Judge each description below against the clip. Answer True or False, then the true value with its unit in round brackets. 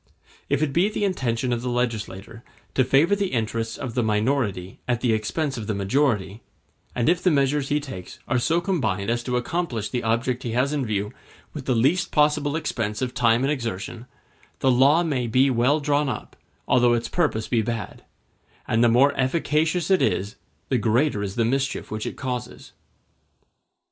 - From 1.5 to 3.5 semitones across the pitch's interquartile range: False (4.1 semitones)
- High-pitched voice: False (125 Hz)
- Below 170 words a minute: False (185 wpm)